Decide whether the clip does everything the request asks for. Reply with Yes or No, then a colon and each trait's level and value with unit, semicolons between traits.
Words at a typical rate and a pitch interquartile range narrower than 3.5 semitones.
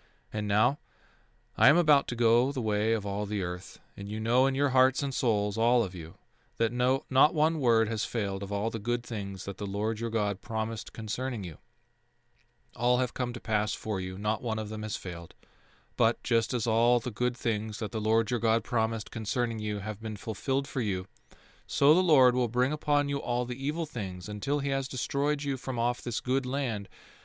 No: fast, 215 wpm; average, 2.9 semitones